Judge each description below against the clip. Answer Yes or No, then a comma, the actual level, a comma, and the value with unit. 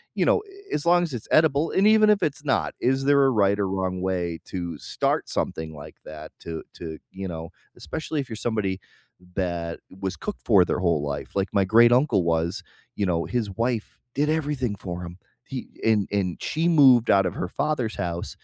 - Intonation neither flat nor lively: No, wide, 7.9 semitones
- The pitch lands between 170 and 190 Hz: No, low, 100 Hz